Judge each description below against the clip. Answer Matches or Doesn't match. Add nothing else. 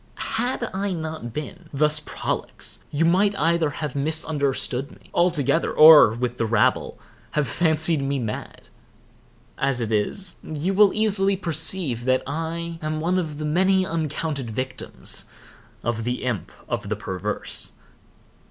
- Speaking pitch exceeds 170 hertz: Doesn't match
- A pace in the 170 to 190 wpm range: Doesn't match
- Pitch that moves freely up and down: Doesn't match